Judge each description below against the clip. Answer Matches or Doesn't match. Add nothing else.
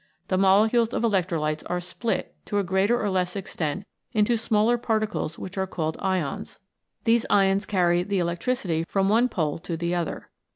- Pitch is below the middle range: Doesn't match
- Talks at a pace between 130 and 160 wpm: Doesn't match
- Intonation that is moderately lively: Matches